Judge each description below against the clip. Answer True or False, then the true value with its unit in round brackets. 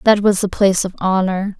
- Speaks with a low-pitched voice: False (195 Hz)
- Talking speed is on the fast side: True (225 wpm)